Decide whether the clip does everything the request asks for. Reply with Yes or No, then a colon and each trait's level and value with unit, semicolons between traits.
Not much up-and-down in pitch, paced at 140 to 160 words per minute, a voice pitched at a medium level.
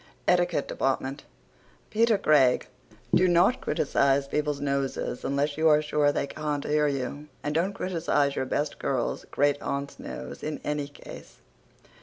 Yes: narrow, 1.8 semitones; average, 155 wpm; medium, 145 Hz